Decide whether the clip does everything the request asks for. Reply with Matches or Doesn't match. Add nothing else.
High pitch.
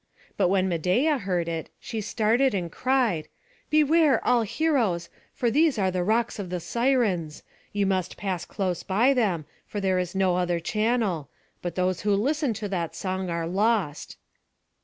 Matches